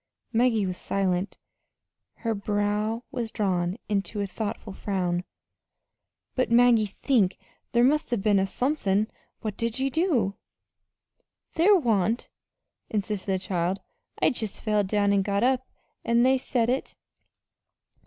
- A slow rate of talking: Yes, slow, 130 wpm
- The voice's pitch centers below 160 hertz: No, high, 215 Hz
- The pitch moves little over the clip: No, average, 3.7 semitones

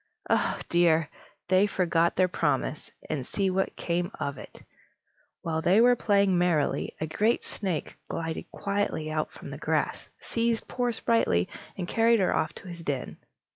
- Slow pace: No, average, 160 wpm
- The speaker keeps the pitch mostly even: No, average, 4.2 semitones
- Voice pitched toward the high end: No, medium, 180 Hz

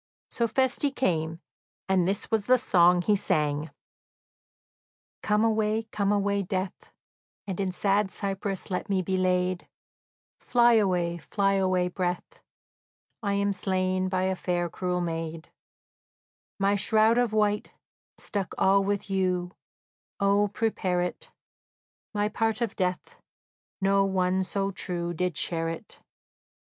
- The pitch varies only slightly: Yes, narrow, 2.3 semitones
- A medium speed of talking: No, slow, 130 wpm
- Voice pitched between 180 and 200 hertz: Yes, high, 190 Hz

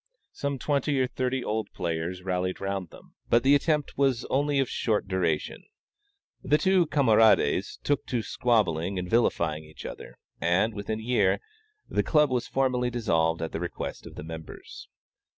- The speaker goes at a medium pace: Yes, average, 165 wpm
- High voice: No, low, 110 Hz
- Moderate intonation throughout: No, wide, 6.7 semitones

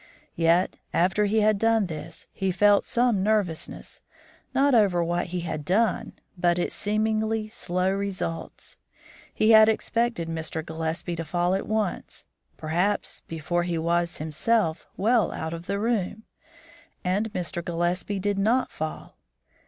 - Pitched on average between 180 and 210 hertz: Yes, medium, 185 Hz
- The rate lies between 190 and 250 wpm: No, average, 140 wpm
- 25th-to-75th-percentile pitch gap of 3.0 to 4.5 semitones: Yes, average, 4.0 semitones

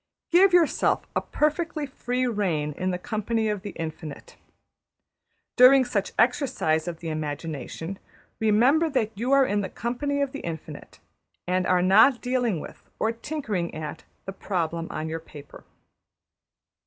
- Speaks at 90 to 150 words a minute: Yes, average, 145 wpm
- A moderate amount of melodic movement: No, wide, 7.4 semitones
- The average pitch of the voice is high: Yes, high, 210 Hz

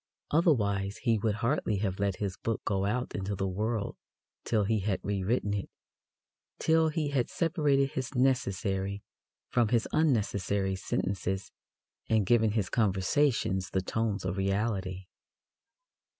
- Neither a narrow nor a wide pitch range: Yes, average, 3.8 semitones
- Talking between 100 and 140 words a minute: Yes, slow, 135 wpm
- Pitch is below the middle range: Yes, low, 105 Hz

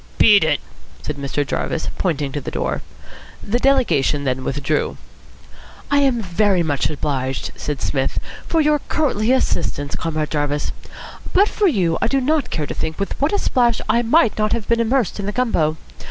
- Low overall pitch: No, high, 195 Hz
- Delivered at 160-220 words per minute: Yes, average, 180 wpm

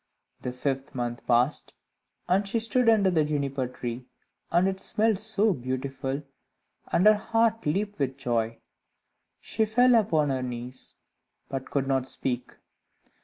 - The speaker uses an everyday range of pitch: No, wide, 8.2 semitones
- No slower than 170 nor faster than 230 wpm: No, average, 140 wpm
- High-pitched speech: No, medium, 140 Hz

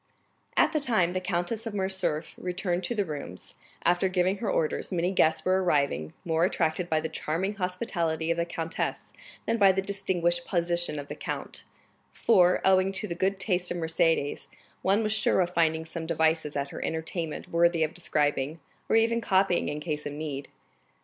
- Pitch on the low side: No, medium, 175 Hz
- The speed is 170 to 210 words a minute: Yes, average, 185 wpm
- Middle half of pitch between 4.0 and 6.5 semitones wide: No, average, 3.0 semitones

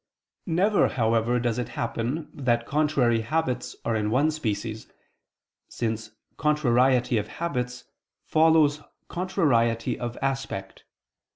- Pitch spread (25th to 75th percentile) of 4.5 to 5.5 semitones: Yes, average, 4.9 semitones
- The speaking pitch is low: Yes, low, 125 Hz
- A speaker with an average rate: No, slow, 105 wpm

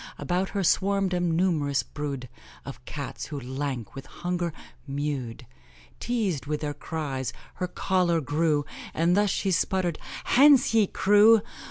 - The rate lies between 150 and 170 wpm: No, average, 140 wpm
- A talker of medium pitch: Yes, medium, 165 Hz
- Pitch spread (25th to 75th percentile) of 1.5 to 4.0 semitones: No, average, 4.9 semitones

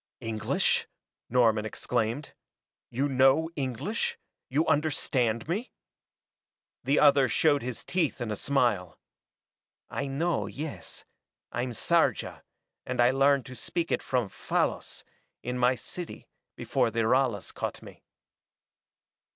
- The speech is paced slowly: Yes, slow, 120 wpm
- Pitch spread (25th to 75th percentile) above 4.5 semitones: No, average, 3.5 semitones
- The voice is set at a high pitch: No, low, 130 Hz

